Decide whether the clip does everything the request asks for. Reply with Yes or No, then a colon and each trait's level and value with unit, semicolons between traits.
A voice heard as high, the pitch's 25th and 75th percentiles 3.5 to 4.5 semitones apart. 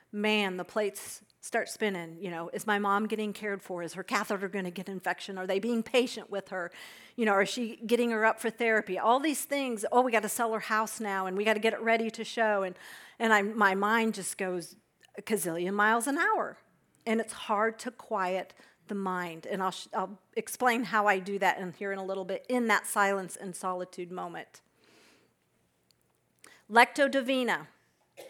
No: high, 210 Hz; average, 3.0 semitones